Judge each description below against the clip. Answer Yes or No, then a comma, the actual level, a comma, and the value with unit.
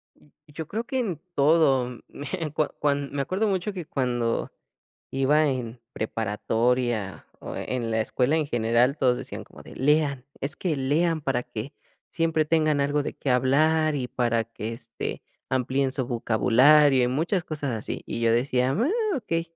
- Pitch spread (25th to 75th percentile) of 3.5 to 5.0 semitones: Yes, average, 4.1 semitones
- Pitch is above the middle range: No, medium, 140 Hz